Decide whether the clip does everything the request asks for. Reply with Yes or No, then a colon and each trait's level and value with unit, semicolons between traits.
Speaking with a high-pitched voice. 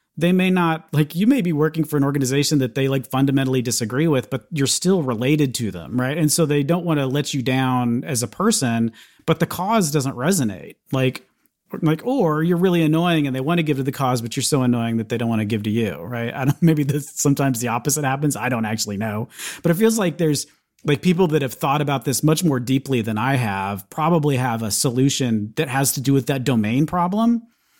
No: medium, 140 Hz